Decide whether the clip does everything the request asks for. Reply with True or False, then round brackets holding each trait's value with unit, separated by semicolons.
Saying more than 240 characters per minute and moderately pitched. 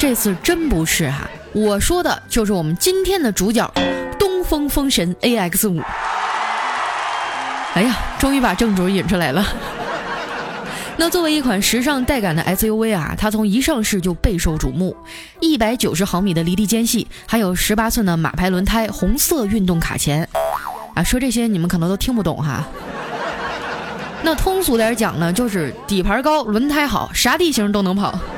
False (260 characters per minute; 215 Hz)